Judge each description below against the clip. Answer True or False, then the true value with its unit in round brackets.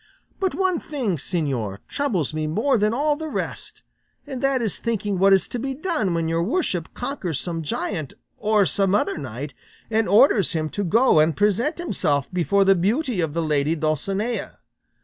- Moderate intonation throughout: False (7.4 semitones)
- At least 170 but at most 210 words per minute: True (180 wpm)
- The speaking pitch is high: True (195 Hz)